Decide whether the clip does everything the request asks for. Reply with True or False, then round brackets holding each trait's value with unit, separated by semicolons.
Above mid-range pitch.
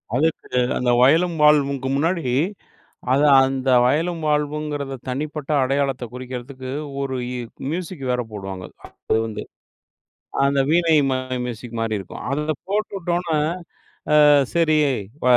False (140 Hz)